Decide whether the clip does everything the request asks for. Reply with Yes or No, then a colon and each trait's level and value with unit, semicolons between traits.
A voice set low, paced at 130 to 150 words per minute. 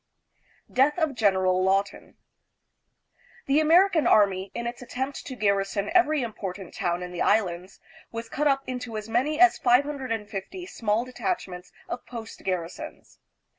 No: high, 230 Hz; slow, 135 wpm